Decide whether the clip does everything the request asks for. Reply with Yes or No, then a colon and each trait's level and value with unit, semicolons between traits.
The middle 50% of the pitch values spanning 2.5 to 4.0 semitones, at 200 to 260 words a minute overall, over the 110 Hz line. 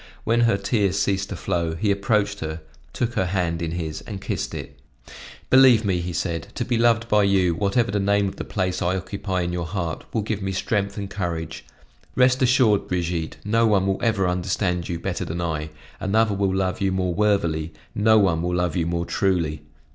No: average, 3.2 semitones; fast, 205 wpm; very low, 95 Hz